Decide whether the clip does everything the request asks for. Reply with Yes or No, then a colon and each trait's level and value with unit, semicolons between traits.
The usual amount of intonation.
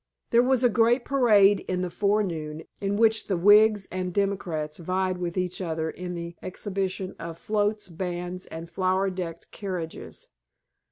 Yes: average, 3.0 semitones